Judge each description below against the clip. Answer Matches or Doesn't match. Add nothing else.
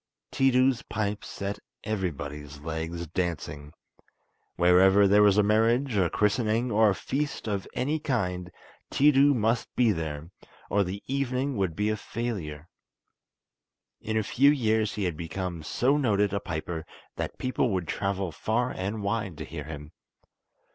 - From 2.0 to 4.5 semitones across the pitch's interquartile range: Doesn't match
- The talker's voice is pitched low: Matches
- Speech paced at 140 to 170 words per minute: Matches